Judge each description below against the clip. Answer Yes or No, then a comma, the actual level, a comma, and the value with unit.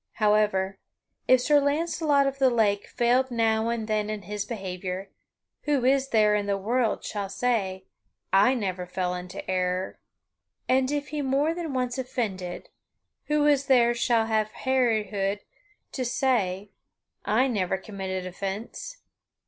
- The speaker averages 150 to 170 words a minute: No, average, 140 wpm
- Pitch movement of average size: Yes, average, 5.0 semitones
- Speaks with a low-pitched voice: No, high, 220 Hz